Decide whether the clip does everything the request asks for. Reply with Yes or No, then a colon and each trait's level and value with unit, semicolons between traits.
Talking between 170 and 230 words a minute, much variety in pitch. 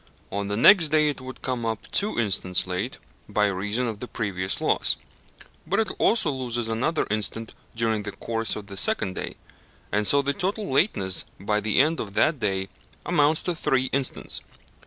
Yes: average, 180 wpm; wide, 5.7 semitones